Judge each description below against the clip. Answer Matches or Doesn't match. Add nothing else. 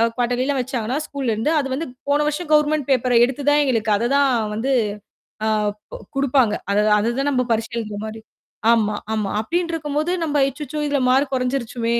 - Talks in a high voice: Matches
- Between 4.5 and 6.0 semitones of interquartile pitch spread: Doesn't match